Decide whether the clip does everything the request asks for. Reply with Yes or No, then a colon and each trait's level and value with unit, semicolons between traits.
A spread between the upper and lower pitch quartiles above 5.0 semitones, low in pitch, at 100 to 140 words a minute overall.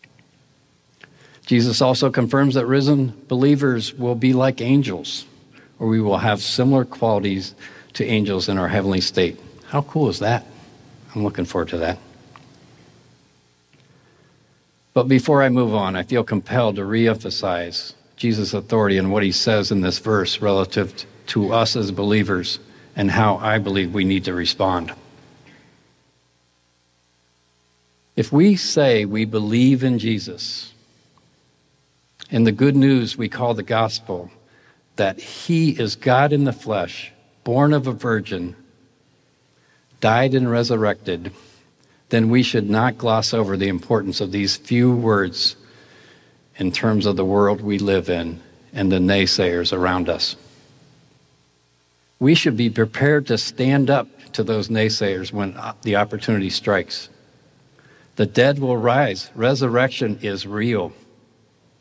No: average, 4.7 semitones; low, 110 Hz; slow, 135 wpm